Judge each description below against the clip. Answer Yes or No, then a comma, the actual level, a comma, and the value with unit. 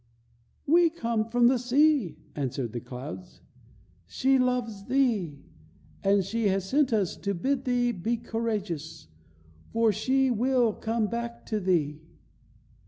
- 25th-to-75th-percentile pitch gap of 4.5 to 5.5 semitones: Yes, average, 4.9 semitones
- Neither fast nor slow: No, slow, 130 wpm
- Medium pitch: No, high, 225 Hz